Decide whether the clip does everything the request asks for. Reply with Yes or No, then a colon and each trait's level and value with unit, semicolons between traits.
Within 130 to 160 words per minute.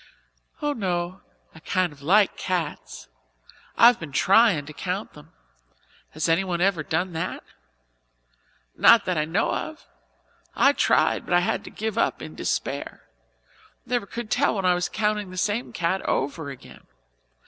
Yes: average, 155 wpm